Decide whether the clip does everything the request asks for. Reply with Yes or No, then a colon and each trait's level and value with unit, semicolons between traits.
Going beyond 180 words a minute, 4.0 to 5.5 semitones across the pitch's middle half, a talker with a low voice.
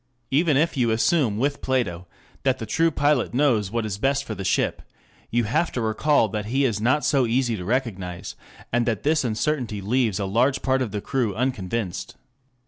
Yes: average, 195 wpm; average, 4.3 semitones; low, 120 Hz